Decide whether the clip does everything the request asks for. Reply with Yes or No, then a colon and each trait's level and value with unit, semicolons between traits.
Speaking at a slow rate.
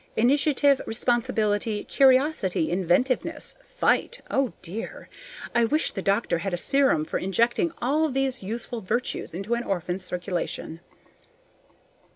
Yes: slow, 120 wpm